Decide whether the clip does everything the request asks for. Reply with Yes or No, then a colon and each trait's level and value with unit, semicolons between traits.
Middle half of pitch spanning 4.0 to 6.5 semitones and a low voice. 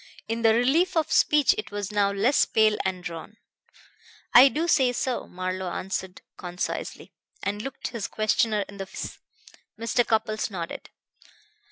No: average, 4.3 semitones; high, 215 Hz